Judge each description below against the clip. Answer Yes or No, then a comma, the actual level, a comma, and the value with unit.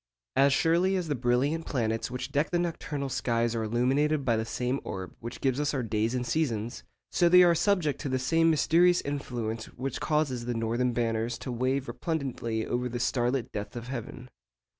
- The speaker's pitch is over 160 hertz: No, low, 130 Hz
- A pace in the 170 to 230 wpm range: Yes, average, 195 wpm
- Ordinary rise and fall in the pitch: Yes, average, 4.2 semitones